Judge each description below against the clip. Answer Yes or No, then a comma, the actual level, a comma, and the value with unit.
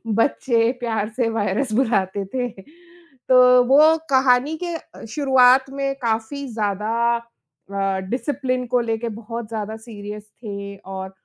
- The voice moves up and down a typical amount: Yes, average, 3.7 semitones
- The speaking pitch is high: Yes, high, 230 Hz